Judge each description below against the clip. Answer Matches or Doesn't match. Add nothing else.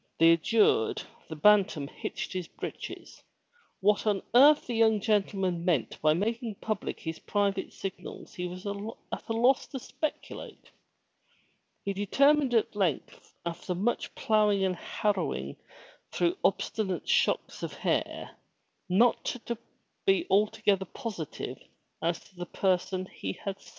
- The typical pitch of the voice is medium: Doesn't match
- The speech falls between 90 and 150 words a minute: Matches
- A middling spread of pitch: Matches